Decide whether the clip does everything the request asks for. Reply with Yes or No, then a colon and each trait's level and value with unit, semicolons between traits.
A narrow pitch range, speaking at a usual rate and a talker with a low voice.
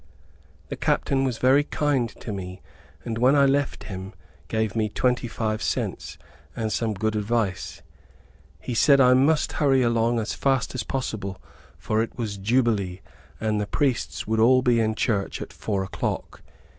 No: average, 3.4 semitones; average, 165 wpm; low, 115 Hz